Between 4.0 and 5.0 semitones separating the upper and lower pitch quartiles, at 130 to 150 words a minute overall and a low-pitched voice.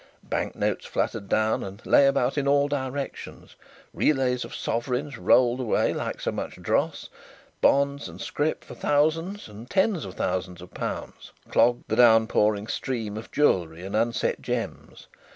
Yes: average, 4.7 semitones; average, 145 wpm; low, 125 Hz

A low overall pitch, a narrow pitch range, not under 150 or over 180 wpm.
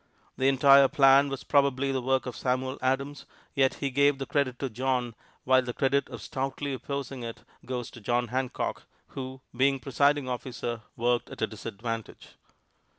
Yes: low, 130 Hz; narrow, 1.8 semitones; average, 165 wpm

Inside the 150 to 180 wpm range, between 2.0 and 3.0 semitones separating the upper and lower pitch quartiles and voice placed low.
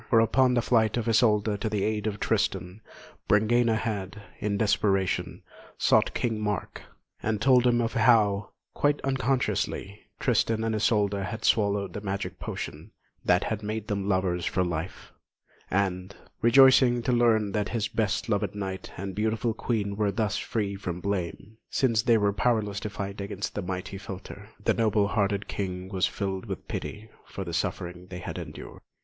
Yes: average, 165 wpm; narrow, 2.4 semitones; low, 105 Hz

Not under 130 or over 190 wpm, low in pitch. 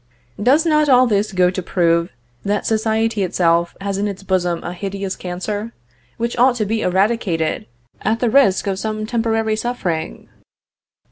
No: average, 155 wpm; high, 205 Hz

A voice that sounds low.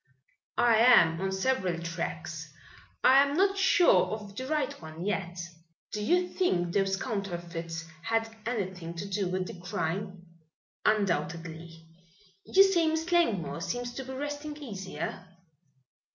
No: high, 200 Hz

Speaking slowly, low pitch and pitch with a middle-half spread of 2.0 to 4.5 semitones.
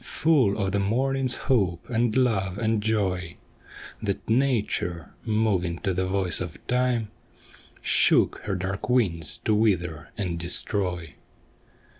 Yes: slow, 125 wpm; low, 100 Hz; average, 4.0 semitones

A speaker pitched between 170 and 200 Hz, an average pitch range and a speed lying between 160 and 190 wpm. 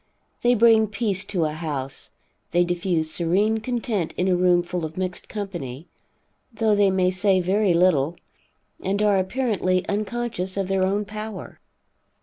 No: high, 190 Hz; average, 3.2 semitones; average, 150 wpm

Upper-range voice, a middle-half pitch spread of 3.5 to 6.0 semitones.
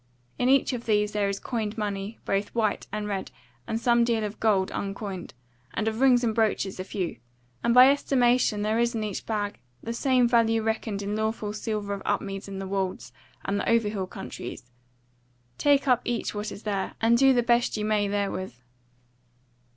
No: high, 215 Hz; average, 2.7 semitones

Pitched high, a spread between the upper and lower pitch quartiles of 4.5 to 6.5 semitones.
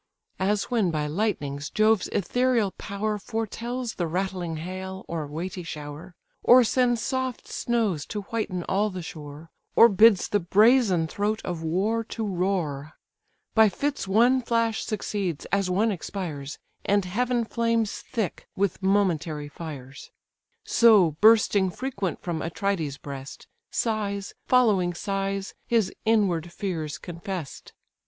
Yes: high, 195 Hz; average, 4.8 semitones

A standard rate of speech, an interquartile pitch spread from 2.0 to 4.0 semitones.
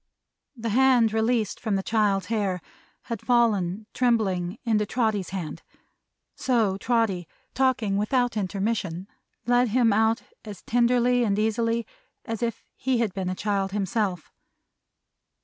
No: slow, 130 wpm; average, 3.1 semitones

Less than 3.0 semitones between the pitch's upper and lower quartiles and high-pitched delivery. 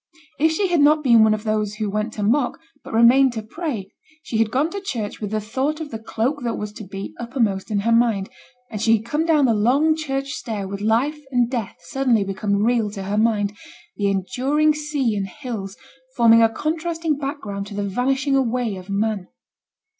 No: average, 4.8 semitones; high, 230 Hz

